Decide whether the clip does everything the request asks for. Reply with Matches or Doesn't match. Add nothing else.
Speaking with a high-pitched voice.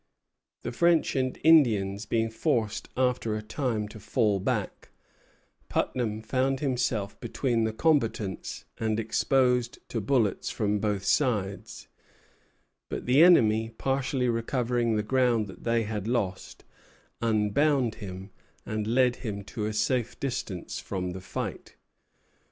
Doesn't match